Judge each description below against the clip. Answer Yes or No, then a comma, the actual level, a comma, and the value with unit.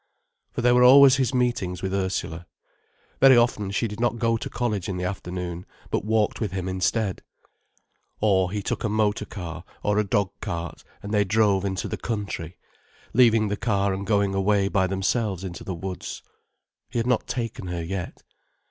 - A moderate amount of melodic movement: Yes, average, 3.3 semitones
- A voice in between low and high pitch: No, low, 100 Hz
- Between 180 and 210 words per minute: Yes, average, 185 wpm